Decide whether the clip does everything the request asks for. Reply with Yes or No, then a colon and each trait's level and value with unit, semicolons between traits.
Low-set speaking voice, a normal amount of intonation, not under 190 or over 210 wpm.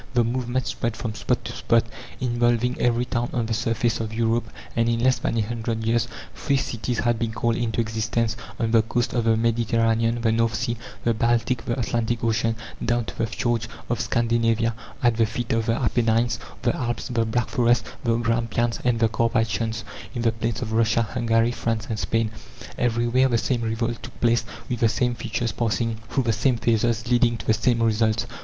No: low, 115 Hz; narrow, 1.0 semitones; average, 200 wpm